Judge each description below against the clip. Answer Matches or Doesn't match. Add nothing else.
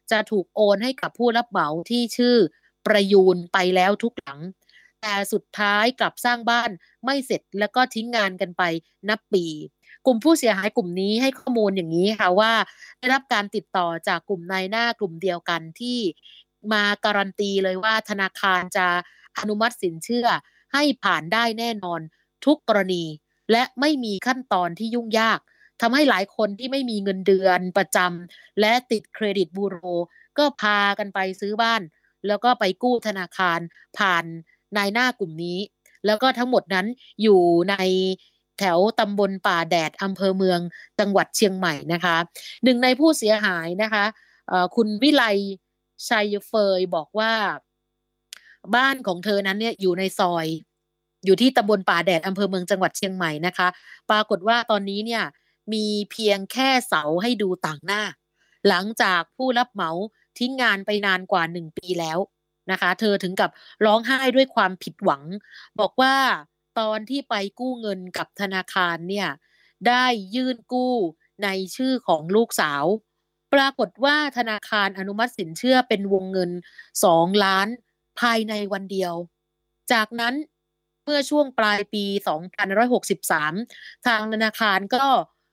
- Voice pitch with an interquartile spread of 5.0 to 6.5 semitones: Doesn't match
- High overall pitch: Matches